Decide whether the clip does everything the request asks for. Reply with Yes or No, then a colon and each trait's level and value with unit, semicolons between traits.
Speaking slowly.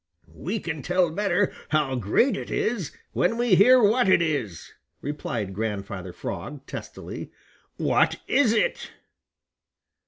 Yes: slow, 125 wpm